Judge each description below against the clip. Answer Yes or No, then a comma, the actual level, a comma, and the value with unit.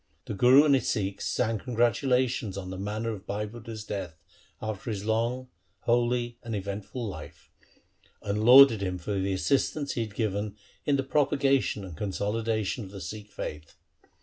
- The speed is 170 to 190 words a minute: Yes, average, 175 wpm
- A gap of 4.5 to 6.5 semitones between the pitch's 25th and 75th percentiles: No, average, 3.5 semitones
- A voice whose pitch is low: Yes, low, 110 Hz